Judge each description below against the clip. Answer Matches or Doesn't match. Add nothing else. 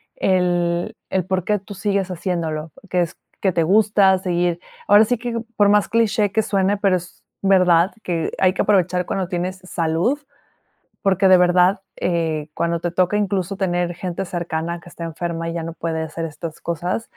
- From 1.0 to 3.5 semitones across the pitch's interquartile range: Matches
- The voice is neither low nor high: Matches